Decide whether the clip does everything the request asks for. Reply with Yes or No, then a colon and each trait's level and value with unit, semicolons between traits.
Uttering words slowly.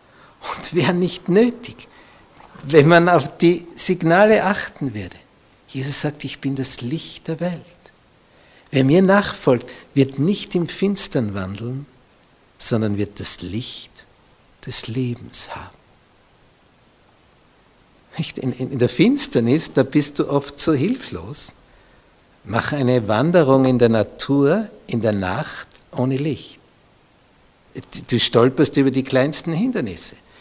Yes: slow, 115 wpm